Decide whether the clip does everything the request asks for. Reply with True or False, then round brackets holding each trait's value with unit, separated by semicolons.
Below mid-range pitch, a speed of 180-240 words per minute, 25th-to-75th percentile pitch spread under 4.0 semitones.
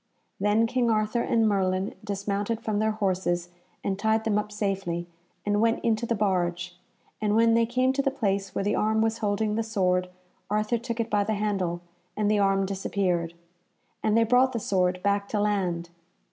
False (210 Hz; 190 wpm; 2.5 semitones)